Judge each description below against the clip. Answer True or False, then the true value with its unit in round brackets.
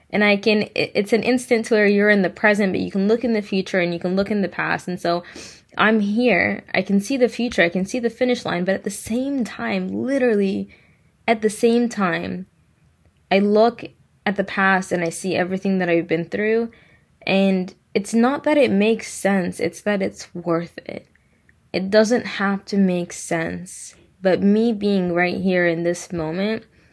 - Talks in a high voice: True (200 Hz)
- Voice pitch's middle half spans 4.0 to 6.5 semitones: False (3.4 semitones)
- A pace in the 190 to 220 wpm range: True (200 wpm)